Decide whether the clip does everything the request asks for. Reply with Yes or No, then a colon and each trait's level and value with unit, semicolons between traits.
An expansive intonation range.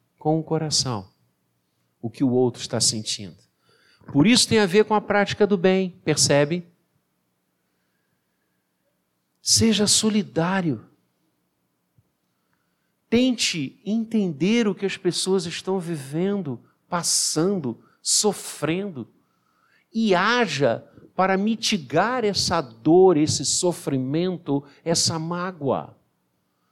Yes: wide, 8.3 semitones